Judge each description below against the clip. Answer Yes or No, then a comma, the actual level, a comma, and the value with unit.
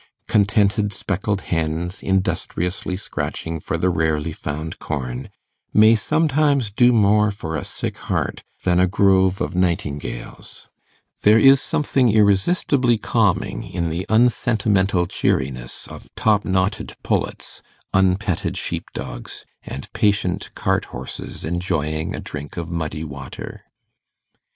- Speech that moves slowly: Yes, slow, 120 wpm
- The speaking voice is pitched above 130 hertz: No, very low, 95 Hz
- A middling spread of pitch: Yes, average, 4.7 semitones